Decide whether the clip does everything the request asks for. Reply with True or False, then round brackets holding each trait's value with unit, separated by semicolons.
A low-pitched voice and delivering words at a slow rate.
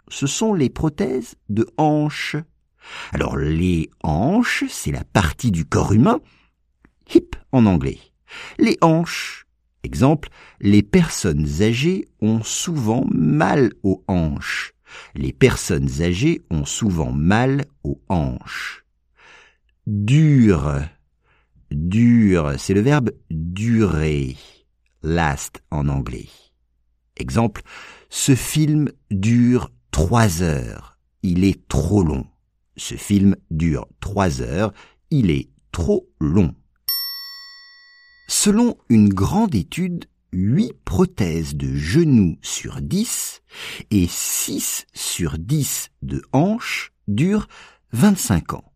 True (105 Hz; 105 wpm)